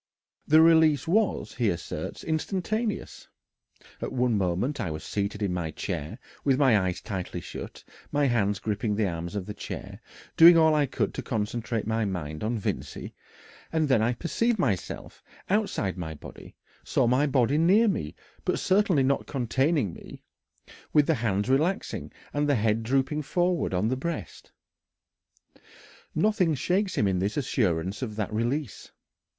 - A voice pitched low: Yes, low, 120 Hz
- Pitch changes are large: Yes, wide, 7.5 semitones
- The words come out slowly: No, average, 155 wpm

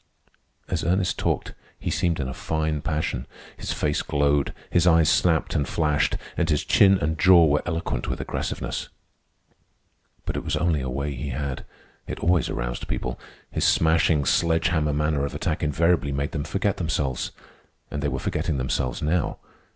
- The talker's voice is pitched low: Yes, very low, 75 Hz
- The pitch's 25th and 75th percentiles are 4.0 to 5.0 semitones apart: No, average, 2.9 semitones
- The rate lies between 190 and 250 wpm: No, average, 170 wpm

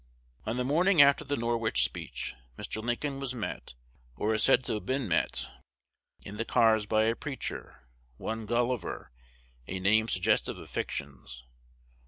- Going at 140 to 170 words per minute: Yes, average, 155 wpm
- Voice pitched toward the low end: Yes, low, 115 Hz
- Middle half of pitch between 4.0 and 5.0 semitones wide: No, average, 3.5 semitones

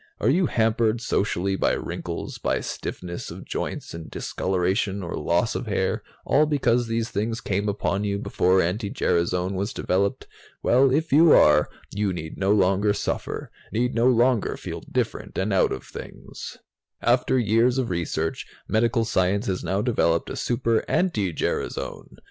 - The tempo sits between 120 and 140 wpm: No, average, 155 wpm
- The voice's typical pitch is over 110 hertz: No, low, 105 Hz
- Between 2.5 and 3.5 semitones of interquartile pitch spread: No, average, 4.0 semitones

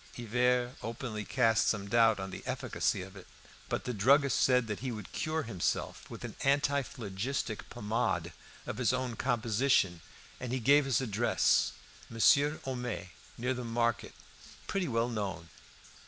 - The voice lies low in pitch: Yes, low, 120 Hz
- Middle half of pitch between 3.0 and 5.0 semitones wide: Yes, average, 3.4 semitones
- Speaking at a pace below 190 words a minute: Yes, average, 150 wpm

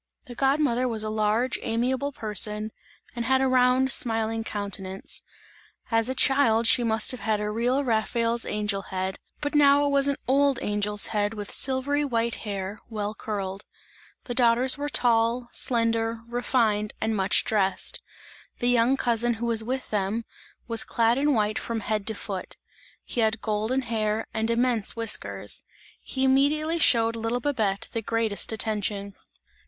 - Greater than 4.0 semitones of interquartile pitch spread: No, average, 3.1 semitones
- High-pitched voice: Yes, high, 230 Hz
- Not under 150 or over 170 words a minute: Yes, average, 160 wpm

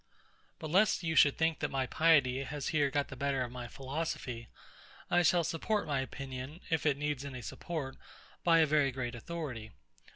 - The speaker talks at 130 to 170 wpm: No, average, 185 wpm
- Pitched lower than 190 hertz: Yes, medium, 140 Hz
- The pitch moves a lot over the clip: No, average, 3.6 semitones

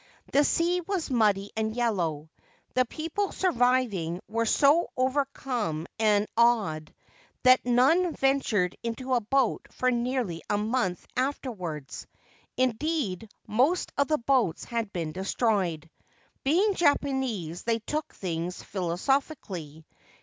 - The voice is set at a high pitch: Yes, high, 235 Hz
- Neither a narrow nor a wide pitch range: No, wide, 6.4 semitones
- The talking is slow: Yes, slow, 115 wpm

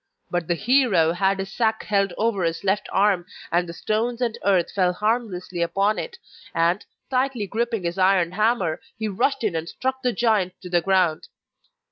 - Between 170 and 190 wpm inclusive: Yes, average, 180 wpm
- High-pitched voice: Yes, high, 195 Hz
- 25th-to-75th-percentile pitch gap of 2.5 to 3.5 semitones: No, average, 4.3 semitones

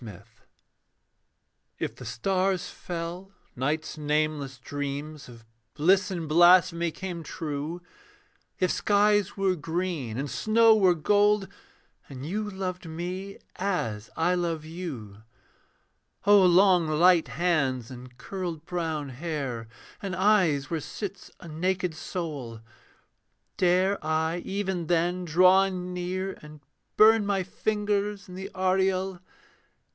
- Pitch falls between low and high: Yes, medium, 175 Hz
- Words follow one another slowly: Yes, slow, 115 wpm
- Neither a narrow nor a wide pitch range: Yes, average, 3.8 semitones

